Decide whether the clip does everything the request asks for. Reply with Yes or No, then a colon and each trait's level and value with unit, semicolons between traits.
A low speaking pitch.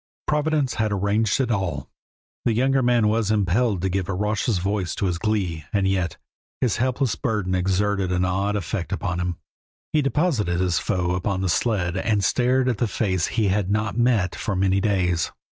Yes: low, 100 Hz